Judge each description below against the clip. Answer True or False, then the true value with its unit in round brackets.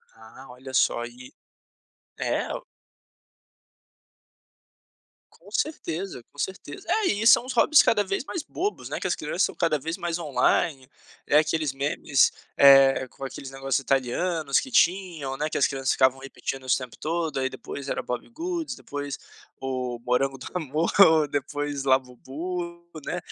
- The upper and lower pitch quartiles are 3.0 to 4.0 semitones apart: False (4.6 semitones)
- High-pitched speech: False (145 Hz)